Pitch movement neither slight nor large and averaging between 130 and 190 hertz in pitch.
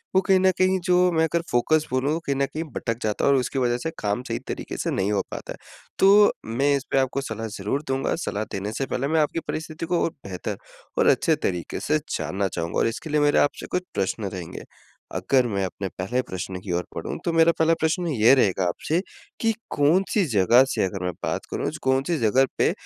No: wide, 7.4 semitones; low, 135 Hz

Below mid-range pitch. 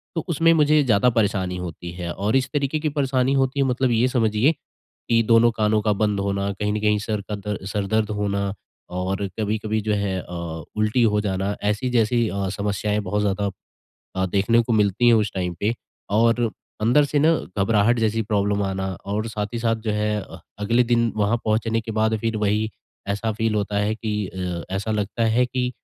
Yes: low, 105 Hz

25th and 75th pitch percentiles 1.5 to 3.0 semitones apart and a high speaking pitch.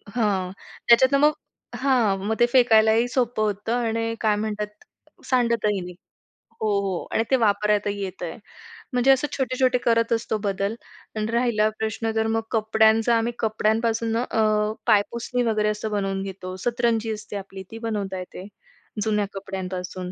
Yes: narrow, 2.4 semitones; high, 220 Hz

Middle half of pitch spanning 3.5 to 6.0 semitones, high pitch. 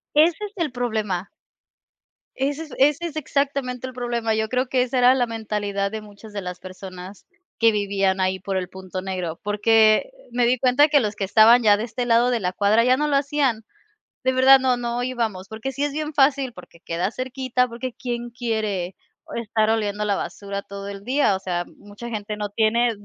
Yes: average, 4.1 semitones; high, 230 Hz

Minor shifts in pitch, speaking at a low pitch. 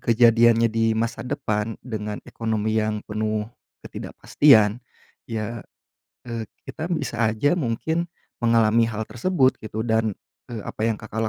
Yes: narrow, 1.4 semitones; low, 115 Hz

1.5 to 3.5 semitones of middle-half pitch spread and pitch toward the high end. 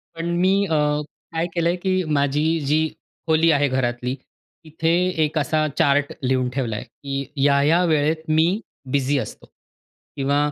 No: average, 2.8 semitones; medium, 145 Hz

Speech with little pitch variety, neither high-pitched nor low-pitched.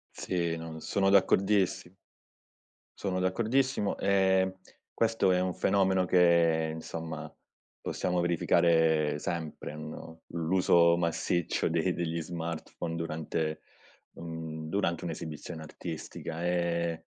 No: narrow, 2.3 semitones; very low, 85 Hz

